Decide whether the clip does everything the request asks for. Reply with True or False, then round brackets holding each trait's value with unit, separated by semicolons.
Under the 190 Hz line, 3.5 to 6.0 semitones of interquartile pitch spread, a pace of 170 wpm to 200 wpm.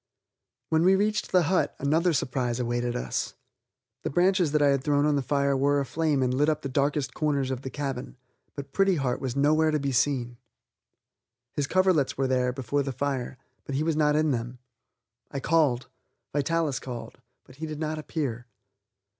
False (140 Hz; 3.0 semitones; 185 wpm)